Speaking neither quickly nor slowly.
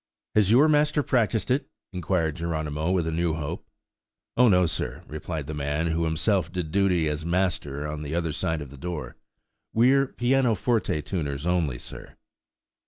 Yes: average, 165 wpm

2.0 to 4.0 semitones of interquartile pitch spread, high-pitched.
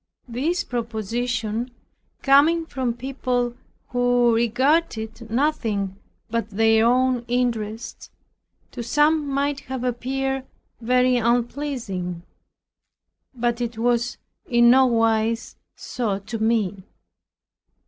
Yes: narrow, 2.4 semitones; high, 240 Hz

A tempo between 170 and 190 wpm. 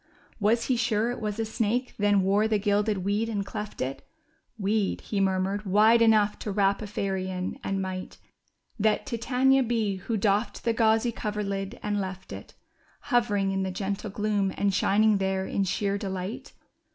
Yes: average, 175 wpm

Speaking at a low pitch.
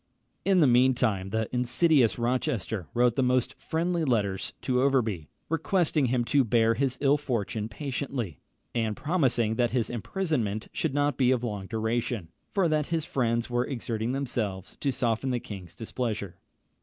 Yes: low, 120 Hz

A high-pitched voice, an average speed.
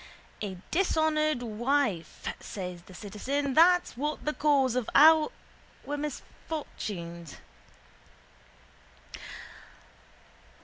No: very high, 275 Hz; slow, 80 wpm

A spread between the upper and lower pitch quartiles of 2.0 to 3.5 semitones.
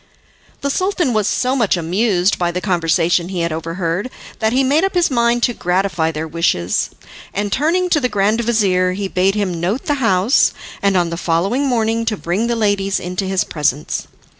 No: average, 5.1 semitones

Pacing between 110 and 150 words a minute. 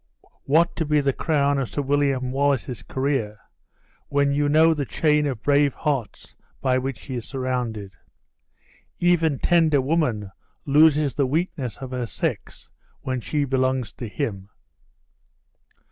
Yes: average, 140 wpm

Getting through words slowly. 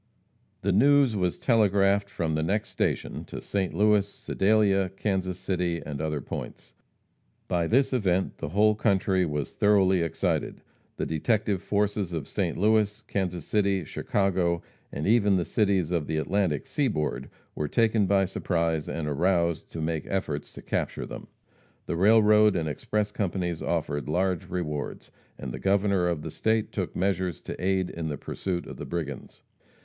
No: average, 160 wpm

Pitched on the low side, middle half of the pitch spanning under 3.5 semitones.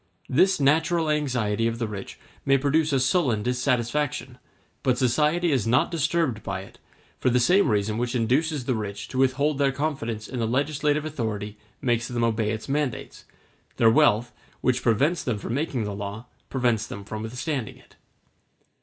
No: low, 125 Hz; average, 4.6 semitones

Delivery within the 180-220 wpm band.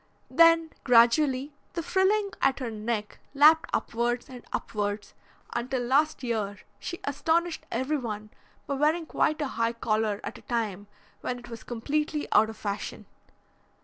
No: average, 145 wpm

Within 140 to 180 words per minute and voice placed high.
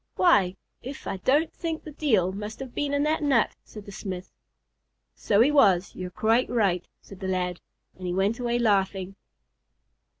Yes: average, 175 wpm; high, 210 Hz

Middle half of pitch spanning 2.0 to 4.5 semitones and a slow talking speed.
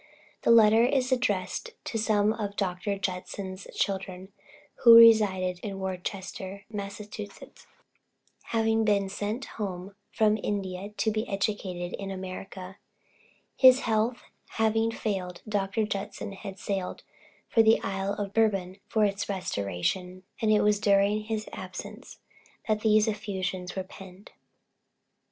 Yes: narrow, 2.4 semitones; slow, 125 wpm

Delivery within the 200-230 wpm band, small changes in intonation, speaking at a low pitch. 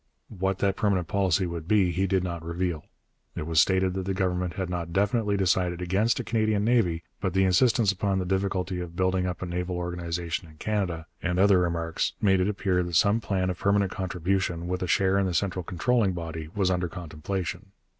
Yes: fast, 205 wpm; narrow, 2.0 semitones; very low, 90 Hz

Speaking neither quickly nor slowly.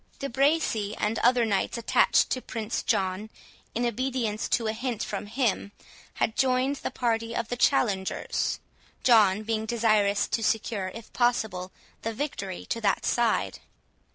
Yes: average, 150 wpm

